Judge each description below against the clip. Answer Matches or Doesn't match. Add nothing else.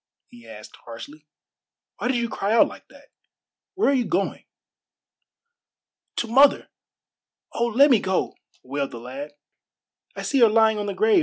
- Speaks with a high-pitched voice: Matches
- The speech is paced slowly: Doesn't match